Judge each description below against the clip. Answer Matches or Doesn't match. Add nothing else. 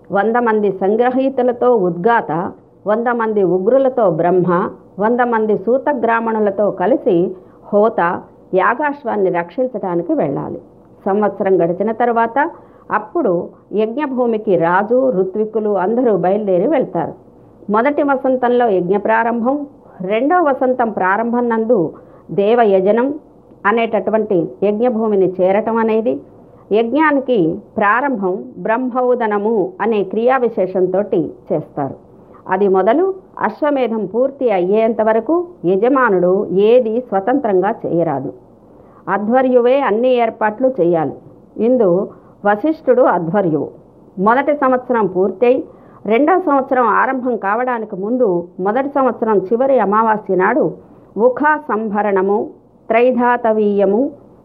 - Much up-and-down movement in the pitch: Doesn't match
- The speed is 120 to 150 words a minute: Doesn't match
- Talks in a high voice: Matches